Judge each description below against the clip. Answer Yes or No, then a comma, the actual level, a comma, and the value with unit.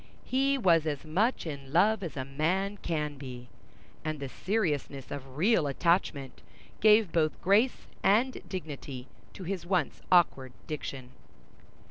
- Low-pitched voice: No, medium, 160 Hz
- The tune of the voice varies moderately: No, wide, 5.9 semitones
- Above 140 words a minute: No, slow, 135 wpm